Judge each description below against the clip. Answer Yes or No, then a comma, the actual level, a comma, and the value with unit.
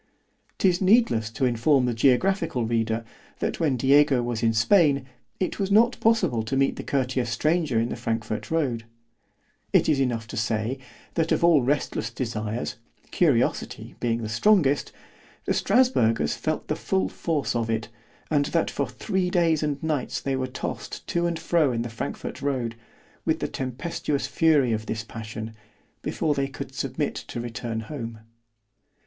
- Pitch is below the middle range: Yes, low, 130 Hz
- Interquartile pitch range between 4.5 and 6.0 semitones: Yes, wide, 5.6 semitones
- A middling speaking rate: Yes, average, 165 wpm